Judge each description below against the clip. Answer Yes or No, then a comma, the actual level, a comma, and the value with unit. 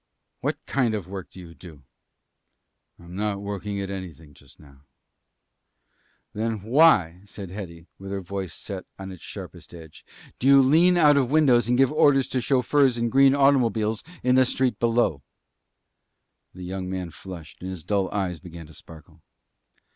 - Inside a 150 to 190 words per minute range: Yes, average, 170 wpm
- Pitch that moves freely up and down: Yes, wide, 6.0 semitones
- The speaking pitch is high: No, low, 100 Hz